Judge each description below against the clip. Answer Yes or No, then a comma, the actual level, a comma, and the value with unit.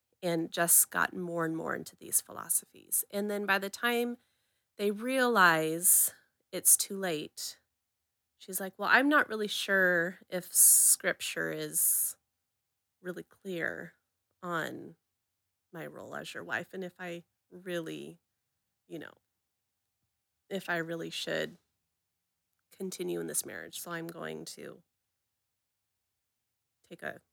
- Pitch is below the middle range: No, medium, 165 Hz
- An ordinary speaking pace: No, slow, 125 wpm